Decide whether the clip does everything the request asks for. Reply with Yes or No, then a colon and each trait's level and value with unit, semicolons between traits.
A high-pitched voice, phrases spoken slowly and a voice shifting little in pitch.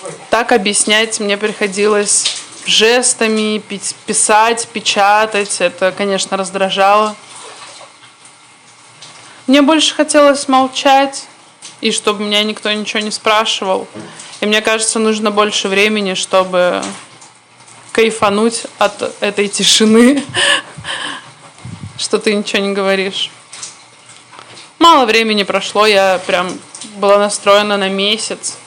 Yes: high, 210 Hz; slow, 95 wpm; narrow, 1.9 semitones